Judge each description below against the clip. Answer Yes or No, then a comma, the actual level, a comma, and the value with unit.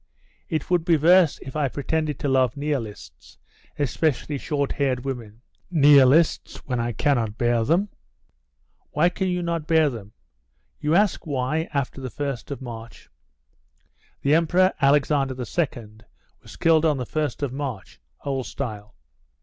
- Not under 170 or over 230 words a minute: No, average, 145 wpm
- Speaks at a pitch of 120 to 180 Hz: Yes, medium, 140 Hz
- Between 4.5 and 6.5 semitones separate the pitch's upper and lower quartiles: No, average, 4.0 semitones